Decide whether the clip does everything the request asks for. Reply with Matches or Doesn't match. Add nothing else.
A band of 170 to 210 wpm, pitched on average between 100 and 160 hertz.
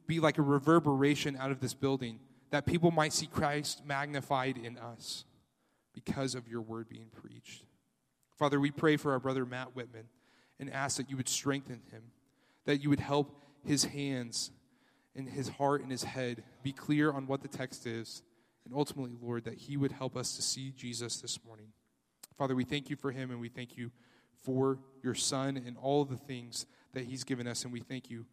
Matches